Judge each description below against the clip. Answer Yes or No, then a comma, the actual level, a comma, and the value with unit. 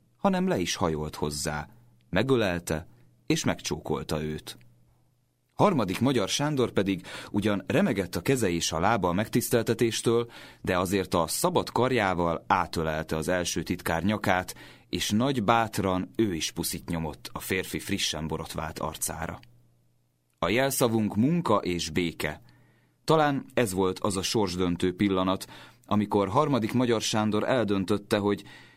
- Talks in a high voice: No, very low, 95 Hz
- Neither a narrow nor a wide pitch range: No, wide, 5.7 semitones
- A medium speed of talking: Yes, average, 130 wpm